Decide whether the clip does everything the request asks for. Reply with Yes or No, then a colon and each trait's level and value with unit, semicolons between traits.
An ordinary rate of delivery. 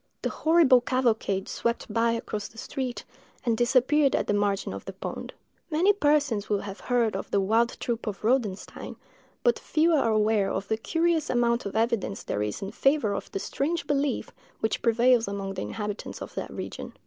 Yes: average, 185 wpm